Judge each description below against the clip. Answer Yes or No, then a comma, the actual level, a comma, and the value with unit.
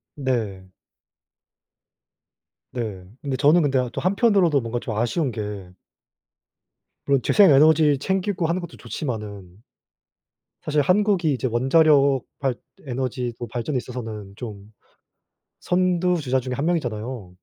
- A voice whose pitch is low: Yes, low, 130 Hz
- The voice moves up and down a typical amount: No, wide, 5.7 semitones